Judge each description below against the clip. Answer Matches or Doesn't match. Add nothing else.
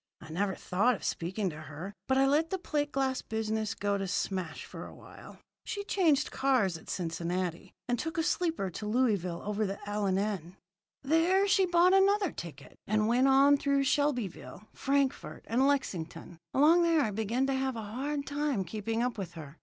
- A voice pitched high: Matches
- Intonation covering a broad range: Matches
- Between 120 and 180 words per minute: Doesn't match